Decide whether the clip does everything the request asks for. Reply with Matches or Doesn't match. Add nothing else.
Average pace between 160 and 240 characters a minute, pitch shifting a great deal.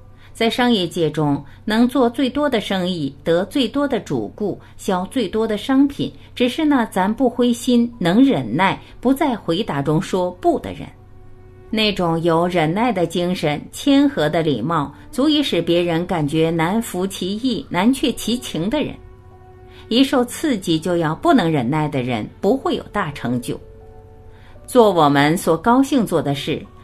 Matches